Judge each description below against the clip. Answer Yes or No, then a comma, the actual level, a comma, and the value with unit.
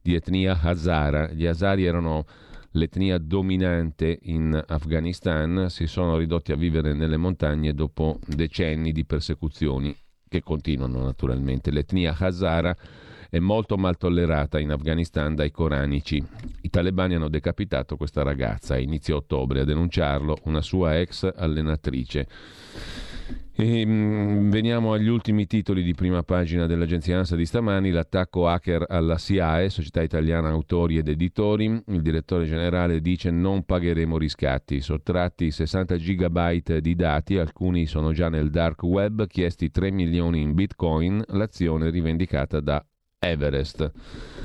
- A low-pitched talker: Yes, very low, 85 Hz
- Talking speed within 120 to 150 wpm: Yes, average, 130 wpm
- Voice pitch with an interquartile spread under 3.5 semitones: Yes, average, 2.7 semitones